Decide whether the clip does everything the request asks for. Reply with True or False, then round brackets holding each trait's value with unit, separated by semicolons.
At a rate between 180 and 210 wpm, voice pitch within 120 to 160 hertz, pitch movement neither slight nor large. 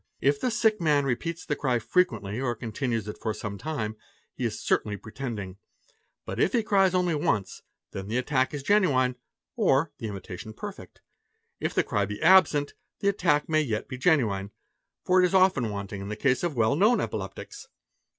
False (190 wpm; 135 Hz; 7.9 semitones)